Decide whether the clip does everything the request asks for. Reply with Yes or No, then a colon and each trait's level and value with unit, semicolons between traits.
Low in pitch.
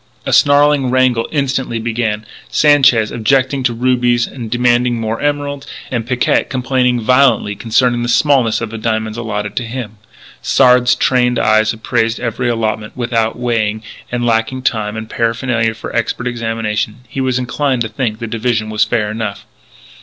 Yes: low, 120 Hz